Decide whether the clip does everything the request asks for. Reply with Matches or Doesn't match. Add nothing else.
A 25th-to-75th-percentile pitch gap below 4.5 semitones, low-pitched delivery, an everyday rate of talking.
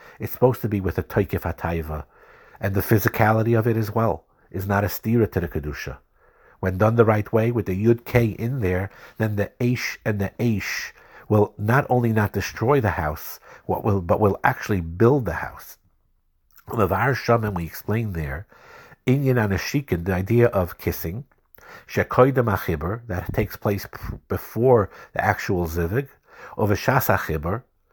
Matches